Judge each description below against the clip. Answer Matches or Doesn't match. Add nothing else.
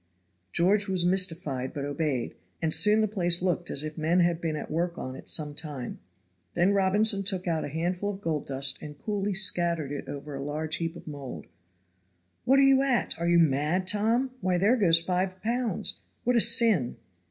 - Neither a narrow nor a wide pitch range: Matches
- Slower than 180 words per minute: Doesn't match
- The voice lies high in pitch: Doesn't match